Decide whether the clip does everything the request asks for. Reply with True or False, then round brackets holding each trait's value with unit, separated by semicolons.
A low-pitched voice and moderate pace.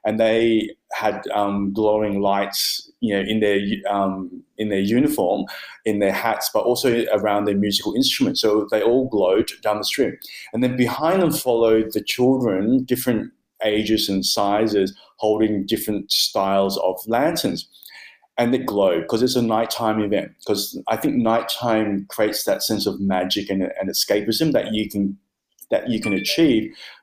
True (110 Hz; 160 wpm)